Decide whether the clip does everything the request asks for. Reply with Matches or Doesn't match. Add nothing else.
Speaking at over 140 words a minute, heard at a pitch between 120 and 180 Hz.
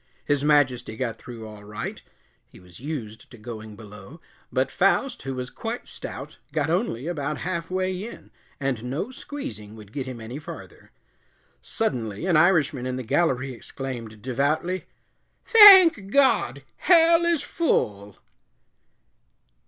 Doesn't match